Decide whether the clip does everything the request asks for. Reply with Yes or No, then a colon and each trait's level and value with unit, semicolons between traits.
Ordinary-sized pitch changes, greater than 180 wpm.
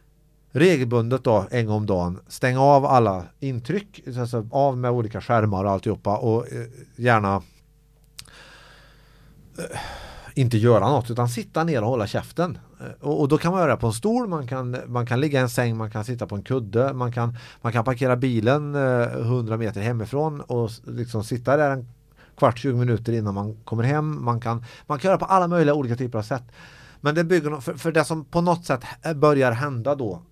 Yes: average, 4.0 semitones; average, 190 wpm